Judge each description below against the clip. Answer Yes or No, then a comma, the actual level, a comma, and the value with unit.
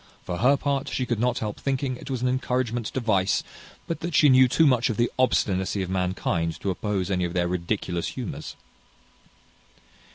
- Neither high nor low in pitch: No, low, 115 Hz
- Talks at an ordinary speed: Yes, average, 190 wpm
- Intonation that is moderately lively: No, wide, 5.7 semitones